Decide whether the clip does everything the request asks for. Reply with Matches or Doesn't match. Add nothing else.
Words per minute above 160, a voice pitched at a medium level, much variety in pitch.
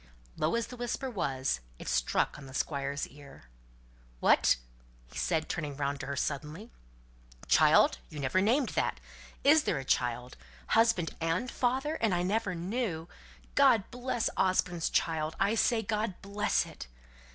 Doesn't match